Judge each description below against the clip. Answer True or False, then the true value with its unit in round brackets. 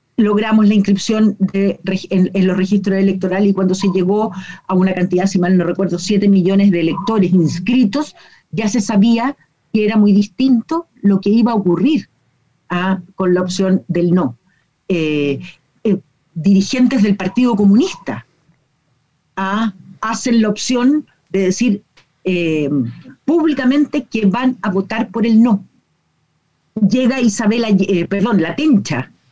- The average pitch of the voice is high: True (195 Hz)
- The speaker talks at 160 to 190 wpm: False (145 wpm)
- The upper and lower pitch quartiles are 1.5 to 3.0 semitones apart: False (3.8 semitones)